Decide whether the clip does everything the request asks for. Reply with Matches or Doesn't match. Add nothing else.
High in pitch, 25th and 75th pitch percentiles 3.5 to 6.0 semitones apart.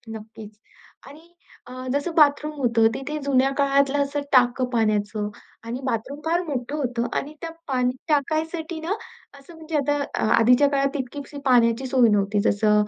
Matches